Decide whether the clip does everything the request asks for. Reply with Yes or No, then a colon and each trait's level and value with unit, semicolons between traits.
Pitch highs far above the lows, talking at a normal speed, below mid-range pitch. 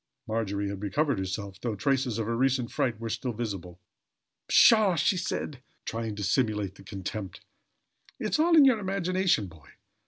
Yes: wide, 6.2 semitones; average, 155 wpm; low, 115 Hz